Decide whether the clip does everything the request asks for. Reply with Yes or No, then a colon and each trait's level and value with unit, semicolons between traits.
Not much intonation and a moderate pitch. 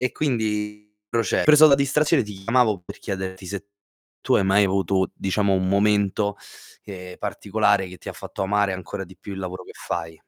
No: narrow, 2.1 semitones; low, 100 Hz